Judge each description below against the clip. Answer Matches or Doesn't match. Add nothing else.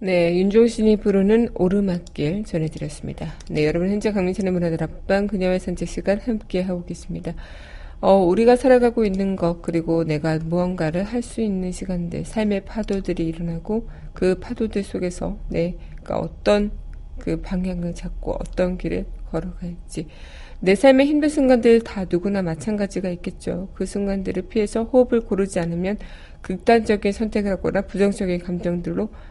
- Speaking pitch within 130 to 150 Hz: Doesn't match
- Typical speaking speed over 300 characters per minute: Matches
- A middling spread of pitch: Matches